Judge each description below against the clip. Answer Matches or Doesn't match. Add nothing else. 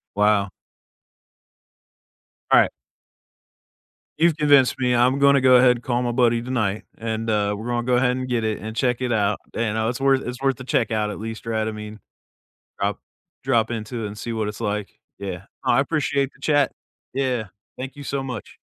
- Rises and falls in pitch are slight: Doesn't match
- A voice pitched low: Matches